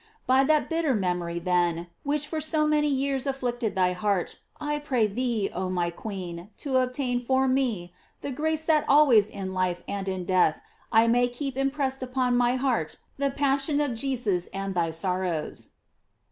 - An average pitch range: No, wide, 6.7 semitones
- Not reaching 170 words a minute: No, average, 175 wpm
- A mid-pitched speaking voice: No, high, 245 Hz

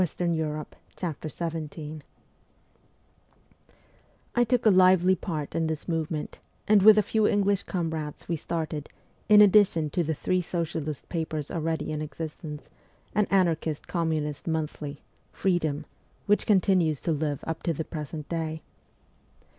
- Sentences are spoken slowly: Yes, slow, 130 wpm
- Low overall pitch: No, medium, 160 Hz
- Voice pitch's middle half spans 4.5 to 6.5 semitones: No, average, 3.1 semitones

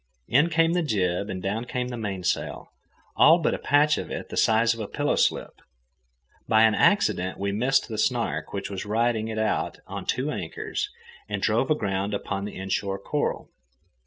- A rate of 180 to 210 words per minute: Yes, average, 185 wpm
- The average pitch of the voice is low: Yes, low, 110 Hz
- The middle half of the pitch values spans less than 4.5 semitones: No, average, 5.2 semitones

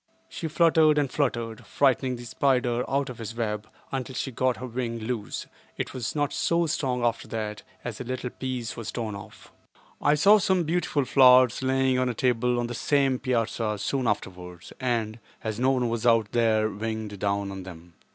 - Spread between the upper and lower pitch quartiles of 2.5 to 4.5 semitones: Yes, average, 3.1 semitones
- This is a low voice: Yes, low, 120 Hz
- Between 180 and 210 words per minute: Yes, average, 190 wpm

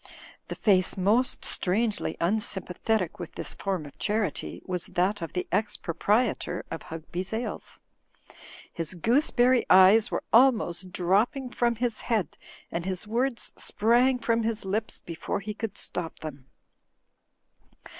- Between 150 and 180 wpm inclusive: No, slow, 135 wpm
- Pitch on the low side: No, high, 205 Hz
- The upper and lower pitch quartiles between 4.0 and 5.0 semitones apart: Yes, average, 4.3 semitones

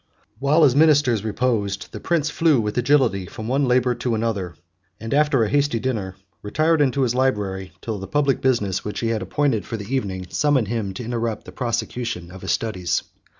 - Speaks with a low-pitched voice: Yes, low, 115 Hz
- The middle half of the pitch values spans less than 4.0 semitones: No, average, 4.7 semitones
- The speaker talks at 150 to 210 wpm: Yes, average, 195 wpm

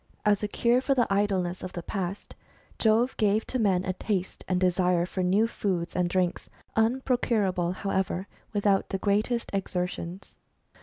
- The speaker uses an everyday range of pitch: Yes, average, 3.1 semitones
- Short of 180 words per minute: Yes, average, 155 wpm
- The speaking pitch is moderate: No, high, 195 Hz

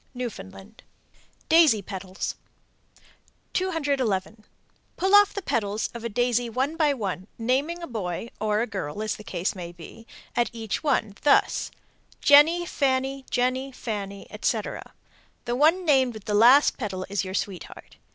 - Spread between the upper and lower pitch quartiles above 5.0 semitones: Yes, wide, 5.6 semitones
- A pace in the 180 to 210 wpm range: No, average, 145 wpm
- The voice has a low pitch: No, high, 235 Hz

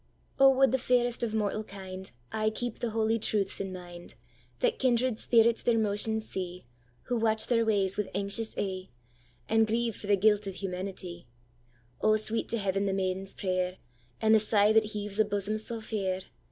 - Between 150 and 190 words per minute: Yes, average, 160 wpm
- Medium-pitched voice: No, high, 205 Hz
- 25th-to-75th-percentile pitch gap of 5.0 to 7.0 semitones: No, average, 3.2 semitones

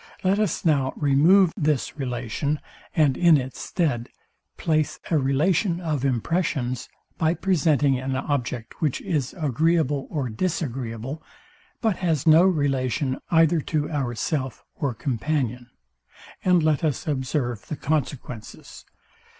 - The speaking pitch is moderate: Yes, medium, 145 Hz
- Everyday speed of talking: No, slow, 120 wpm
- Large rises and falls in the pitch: No, average, 3.9 semitones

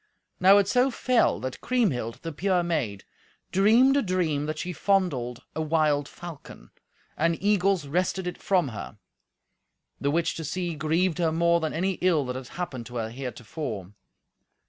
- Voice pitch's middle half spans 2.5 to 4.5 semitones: No, average, 4.9 semitones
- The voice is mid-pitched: Yes, medium, 165 Hz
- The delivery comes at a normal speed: Yes, average, 165 wpm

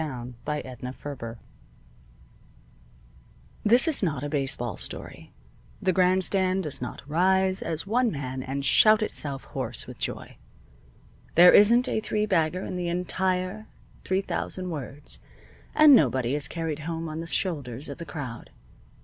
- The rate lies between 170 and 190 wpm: No, average, 150 wpm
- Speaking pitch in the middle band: Yes, medium, 165 Hz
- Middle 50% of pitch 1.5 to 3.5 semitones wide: No, average, 5.1 semitones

